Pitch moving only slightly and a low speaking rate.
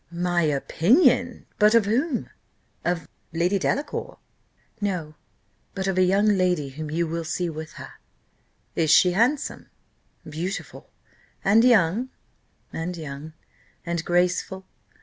No: average, 4.4 semitones; slow, 120 wpm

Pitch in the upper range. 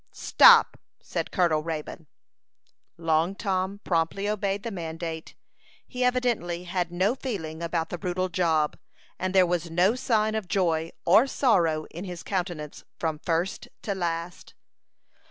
No: medium, 175 Hz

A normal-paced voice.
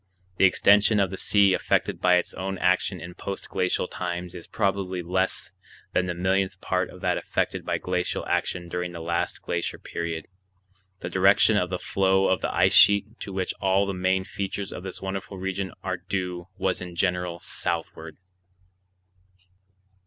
Yes: average, 170 wpm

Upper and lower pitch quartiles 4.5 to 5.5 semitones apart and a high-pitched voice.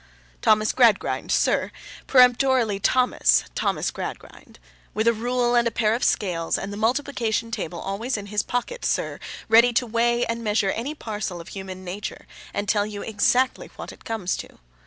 No: average, 3.1 semitones; high, 225 Hz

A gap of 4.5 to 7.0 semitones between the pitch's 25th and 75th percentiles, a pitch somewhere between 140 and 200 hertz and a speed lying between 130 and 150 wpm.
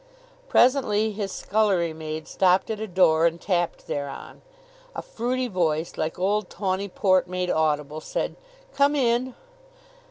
Yes: average, 5.1 semitones; medium, 185 Hz; slow, 135 wpm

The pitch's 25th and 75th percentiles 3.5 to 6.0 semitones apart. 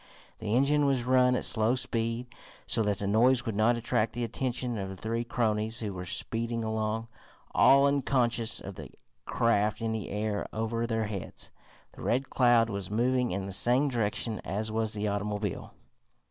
No: narrow, 2.4 semitones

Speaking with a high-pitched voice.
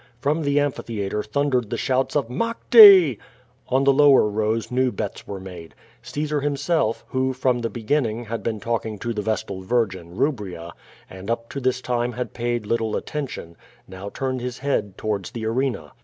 No: low, 120 Hz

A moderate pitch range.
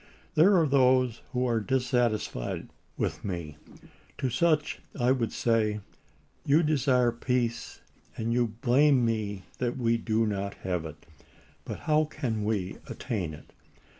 Yes: average, 3.4 semitones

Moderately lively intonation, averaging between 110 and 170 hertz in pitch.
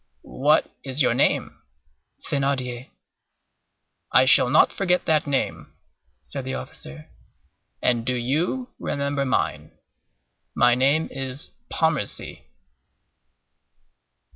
Yes: average, 3.1 semitones; low, 135 Hz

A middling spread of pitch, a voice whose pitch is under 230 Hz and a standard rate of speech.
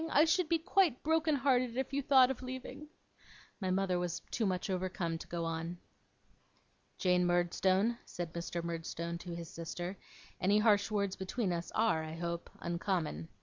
No: wide, 6.4 semitones; medium, 185 Hz; average, 170 wpm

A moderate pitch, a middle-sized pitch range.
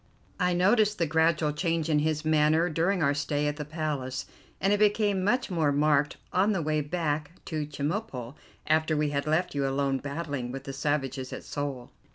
Yes: medium, 150 Hz; average, 3.0 semitones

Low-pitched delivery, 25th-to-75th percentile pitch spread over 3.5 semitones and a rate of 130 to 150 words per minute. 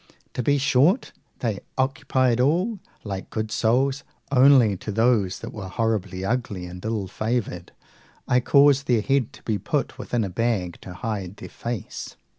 No: low, 115 Hz; average, 4.7 semitones; average, 160 wpm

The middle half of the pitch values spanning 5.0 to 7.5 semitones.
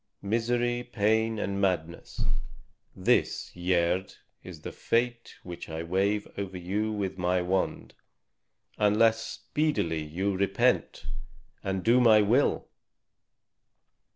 No: average, 3.7 semitones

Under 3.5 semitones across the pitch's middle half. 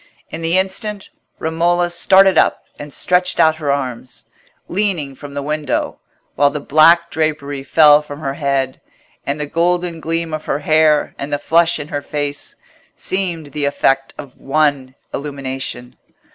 Yes: average, 3.0 semitones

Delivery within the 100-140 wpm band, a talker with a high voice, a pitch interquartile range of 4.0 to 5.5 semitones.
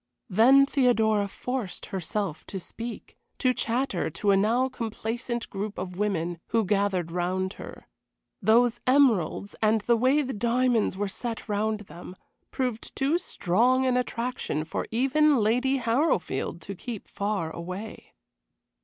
Yes: slow, 135 wpm; high, 220 Hz; average, 4.4 semitones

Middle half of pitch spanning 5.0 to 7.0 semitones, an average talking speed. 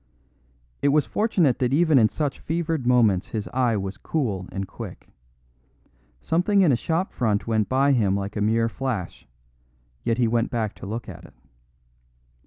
Yes: wide, 5.4 semitones; average, 170 wpm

